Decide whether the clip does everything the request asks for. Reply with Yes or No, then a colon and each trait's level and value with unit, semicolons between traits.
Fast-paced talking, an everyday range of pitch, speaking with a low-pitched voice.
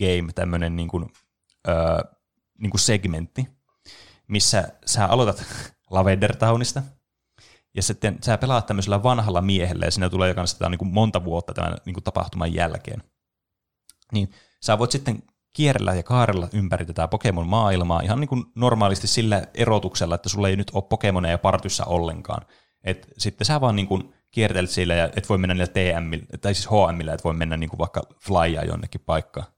Yes: fast, 170 wpm; average, 3.7 semitones; very low, 95 Hz